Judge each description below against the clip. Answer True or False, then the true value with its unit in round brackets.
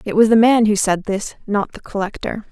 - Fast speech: True (240 wpm)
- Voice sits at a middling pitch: False (210 Hz)